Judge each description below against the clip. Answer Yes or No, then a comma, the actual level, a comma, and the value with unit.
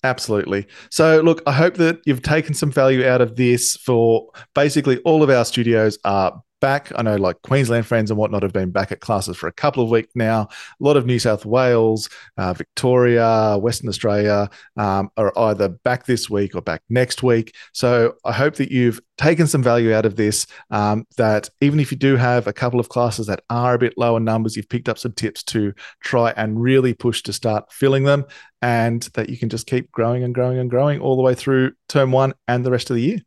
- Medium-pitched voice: No, low, 120 Hz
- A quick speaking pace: Yes, fast, 225 wpm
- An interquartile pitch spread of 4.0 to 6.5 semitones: No, average, 3.0 semitones